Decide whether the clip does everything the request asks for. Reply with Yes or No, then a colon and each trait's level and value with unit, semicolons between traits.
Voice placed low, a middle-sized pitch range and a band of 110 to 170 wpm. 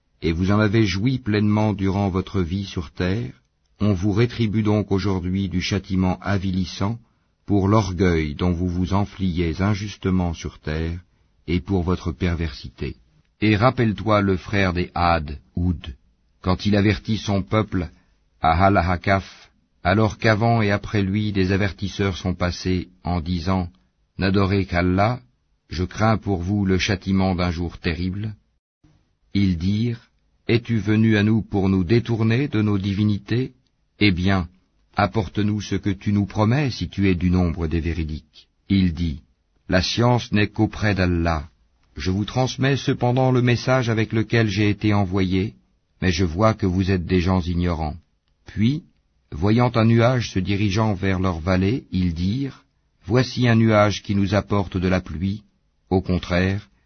Yes: very low, 95 Hz; average, 3.1 semitones; average, 150 wpm